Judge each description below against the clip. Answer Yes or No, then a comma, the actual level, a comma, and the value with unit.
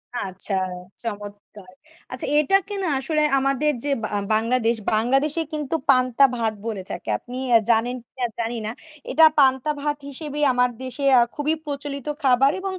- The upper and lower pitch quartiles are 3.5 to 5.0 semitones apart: Yes, average, 4.3 semitones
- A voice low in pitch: No, very high, 260 Hz